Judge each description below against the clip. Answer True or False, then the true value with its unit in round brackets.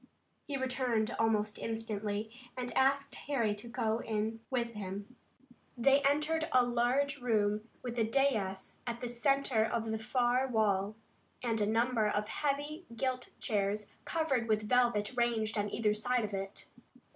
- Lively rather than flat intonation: False (3.2 semitones)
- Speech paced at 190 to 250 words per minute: False (150 wpm)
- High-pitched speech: True (230 Hz)